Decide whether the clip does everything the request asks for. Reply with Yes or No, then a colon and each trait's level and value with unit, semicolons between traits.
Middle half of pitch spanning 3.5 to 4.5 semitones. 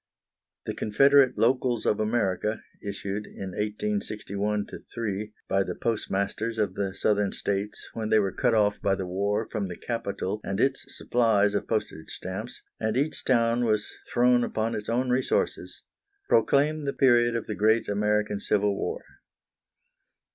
No: average, 2.8 semitones